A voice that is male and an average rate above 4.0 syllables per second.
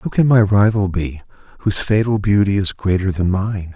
Yes: male; 5.5 syllables/s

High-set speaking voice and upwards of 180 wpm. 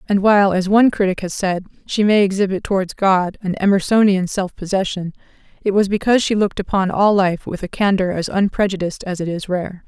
Yes: high, 195 Hz; average, 200 wpm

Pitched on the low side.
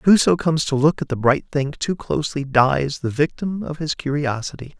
No: medium, 145 Hz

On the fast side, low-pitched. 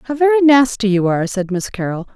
No: fast, 225 wpm; high, 225 Hz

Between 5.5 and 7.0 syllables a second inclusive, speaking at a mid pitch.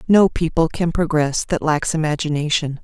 No: 4.9 syllables/s; medium, 160 Hz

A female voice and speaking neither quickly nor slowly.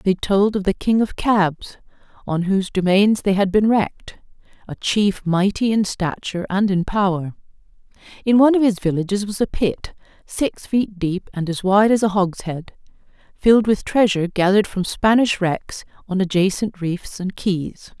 Yes: female; average, 170 wpm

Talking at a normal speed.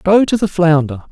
No: fast, 215 wpm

